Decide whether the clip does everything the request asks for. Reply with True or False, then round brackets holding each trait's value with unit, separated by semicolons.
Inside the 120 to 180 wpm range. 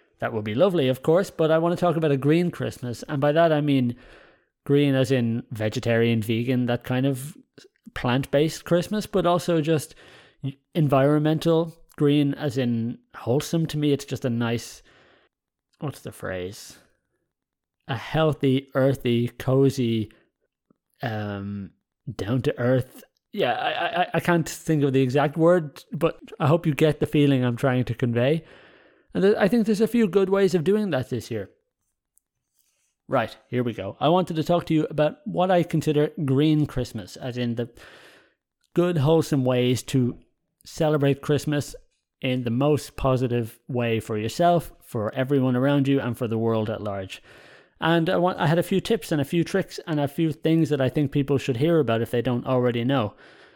True (175 wpm)